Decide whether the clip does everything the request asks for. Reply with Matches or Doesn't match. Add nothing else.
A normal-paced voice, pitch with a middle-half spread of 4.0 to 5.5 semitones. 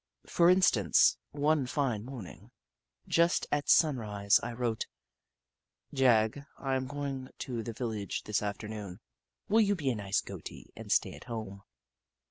Matches